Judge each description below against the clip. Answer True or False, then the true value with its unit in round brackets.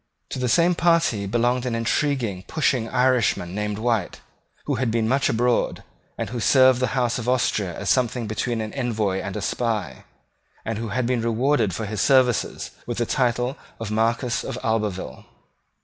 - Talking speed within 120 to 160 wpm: False (175 wpm)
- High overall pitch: False (115 Hz)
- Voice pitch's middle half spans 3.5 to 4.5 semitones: False (2.7 semitones)